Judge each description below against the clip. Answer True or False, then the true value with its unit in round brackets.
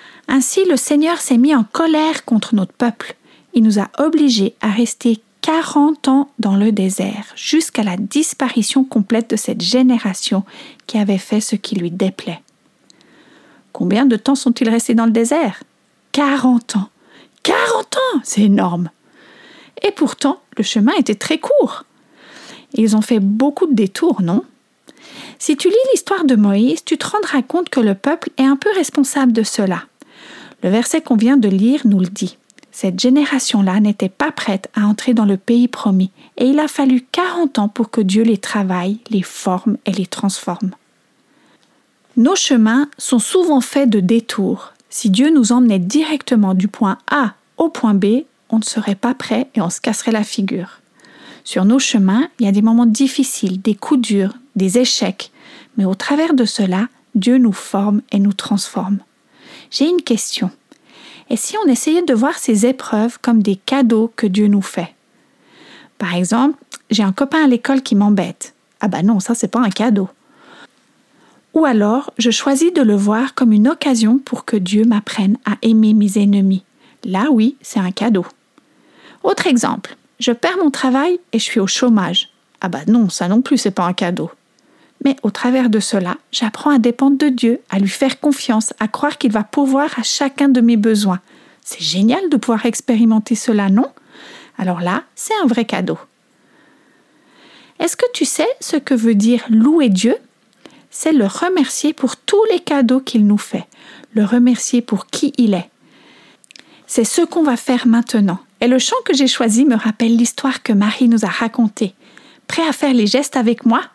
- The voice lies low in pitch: False (240 Hz)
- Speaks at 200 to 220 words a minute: False (180 wpm)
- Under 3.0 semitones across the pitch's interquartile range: False (4.9 semitones)